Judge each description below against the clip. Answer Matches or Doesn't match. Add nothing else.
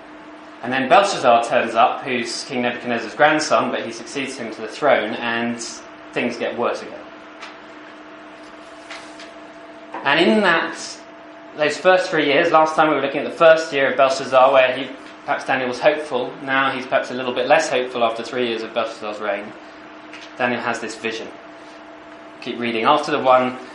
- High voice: Doesn't match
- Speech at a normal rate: Matches